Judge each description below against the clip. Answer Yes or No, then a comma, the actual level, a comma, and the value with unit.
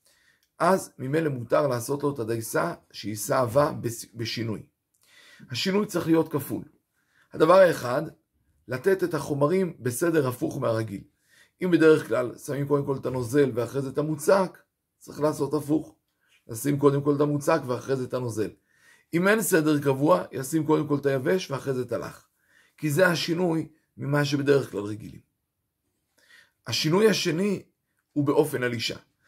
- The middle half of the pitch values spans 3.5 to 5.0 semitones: Yes, average, 4.1 semitones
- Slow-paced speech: No, average, 145 wpm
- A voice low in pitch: No, medium, 145 Hz